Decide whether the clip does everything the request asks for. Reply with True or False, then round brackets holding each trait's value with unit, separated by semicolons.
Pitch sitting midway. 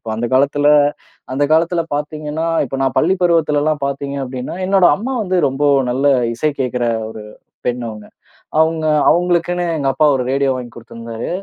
True (145 Hz)